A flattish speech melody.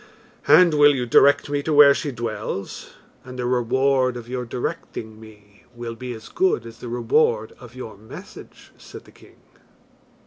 No: average, 3.4 semitones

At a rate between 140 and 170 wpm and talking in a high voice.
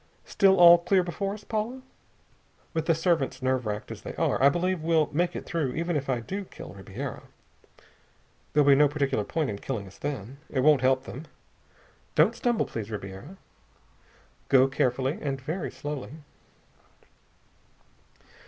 No: average, 155 wpm; medium, 145 Hz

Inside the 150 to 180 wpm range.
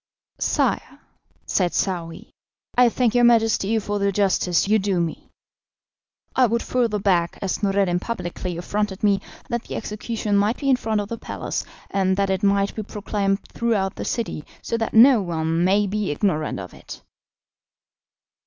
Yes: average, 160 wpm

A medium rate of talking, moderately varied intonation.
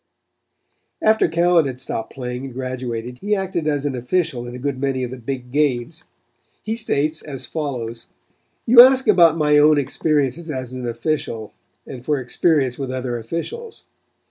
Yes: average, 165 wpm; average, 4.4 semitones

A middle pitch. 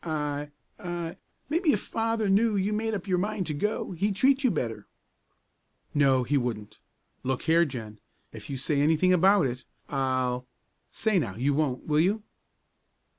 Yes: medium, 160 Hz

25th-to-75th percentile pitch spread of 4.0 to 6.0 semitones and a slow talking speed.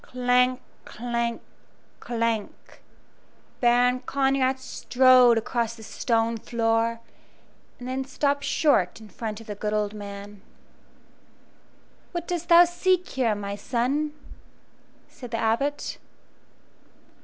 No: average, 2.9 semitones; slow, 110 wpm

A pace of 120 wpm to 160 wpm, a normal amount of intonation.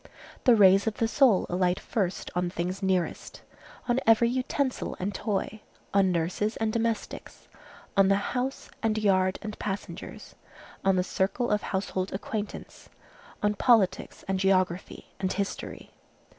Yes: average, 140 wpm; average, 3.0 semitones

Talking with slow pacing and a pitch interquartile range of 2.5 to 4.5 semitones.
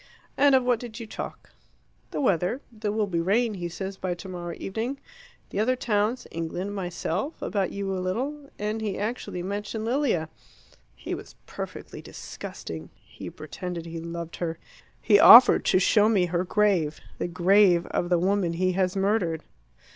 No: average, 165 wpm; average, 3.9 semitones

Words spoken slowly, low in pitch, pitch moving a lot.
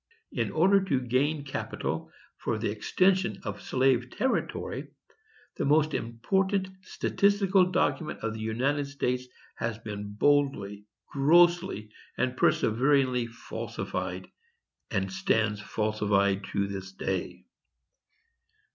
Yes: slow, 105 wpm; low, 125 Hz; wide, 6.6 semitones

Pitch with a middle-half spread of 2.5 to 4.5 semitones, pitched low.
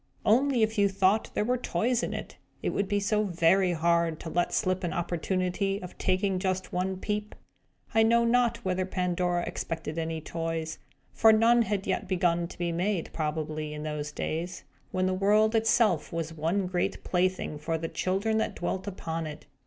No: average, 3.8 semitones; medium, 185 Hz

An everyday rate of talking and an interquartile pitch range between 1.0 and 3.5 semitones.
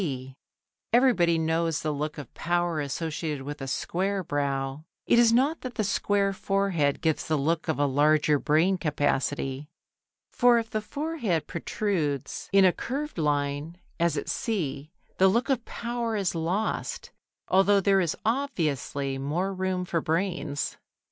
No: average, 150 wpm; average, 5.3 semitones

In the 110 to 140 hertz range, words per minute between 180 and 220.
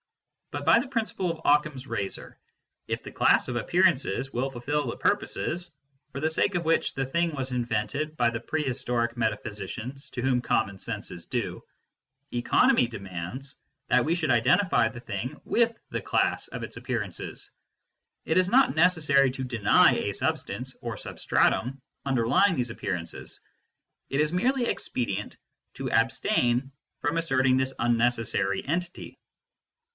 No: low, 135 Hz; average, 150 wpm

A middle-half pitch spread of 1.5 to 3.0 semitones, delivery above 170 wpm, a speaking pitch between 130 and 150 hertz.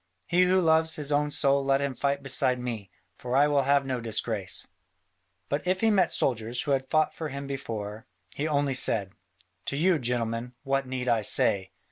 No: average, 3.4 semitones; average, 190 wpm; low, 135 Hz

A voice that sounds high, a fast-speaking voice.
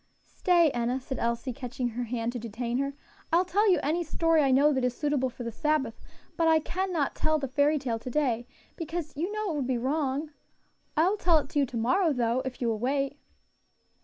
Yes: very high, 275 Hz; fast, 225 wpm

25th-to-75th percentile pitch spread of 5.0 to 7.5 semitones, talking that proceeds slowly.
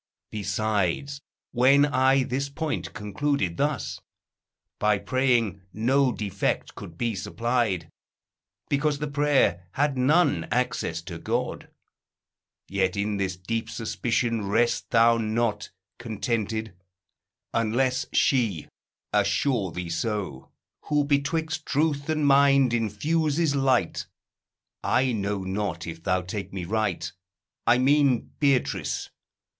Yes: wide, 5.5 semitones; slow, 110 wpm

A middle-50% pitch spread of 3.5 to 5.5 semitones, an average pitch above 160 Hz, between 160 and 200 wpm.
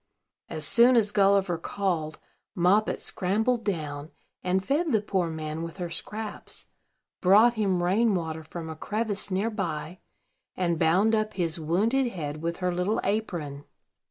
No: average, 4.6 semitones; medium, 185 Hz; average, 150 wpm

